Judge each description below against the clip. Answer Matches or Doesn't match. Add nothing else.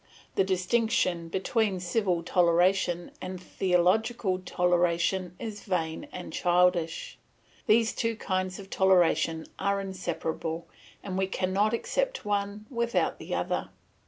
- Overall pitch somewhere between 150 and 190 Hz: Matches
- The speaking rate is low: Matches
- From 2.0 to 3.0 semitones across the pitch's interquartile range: Matches